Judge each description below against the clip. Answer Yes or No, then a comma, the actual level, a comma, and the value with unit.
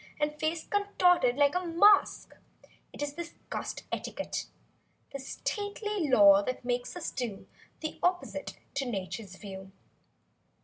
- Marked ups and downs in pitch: Yes, wide, 6.6 semitones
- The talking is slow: Yes, slow, 130 wpm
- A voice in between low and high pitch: No, very high, 290 Hz